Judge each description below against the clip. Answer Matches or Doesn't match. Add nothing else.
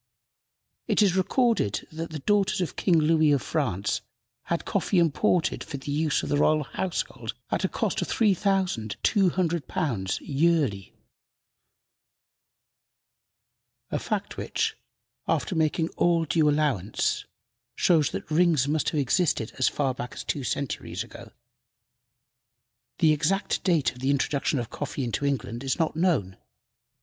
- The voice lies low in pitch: Doesn't match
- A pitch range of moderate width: Matches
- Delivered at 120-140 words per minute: Matches